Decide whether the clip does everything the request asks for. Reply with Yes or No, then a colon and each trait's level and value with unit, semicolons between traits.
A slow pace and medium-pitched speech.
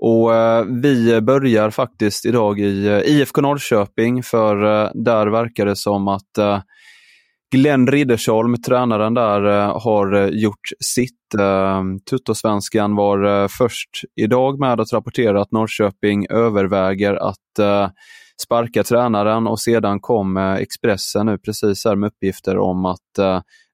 No: slow, 115 wpm; low, 110 Hz